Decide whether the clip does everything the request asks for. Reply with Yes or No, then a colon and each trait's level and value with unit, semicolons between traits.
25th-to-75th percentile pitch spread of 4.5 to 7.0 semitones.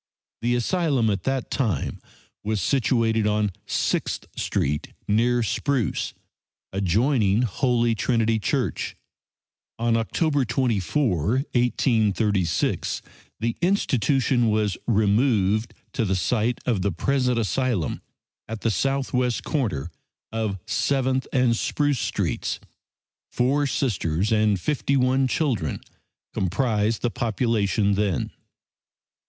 No: average, 3.8 semitones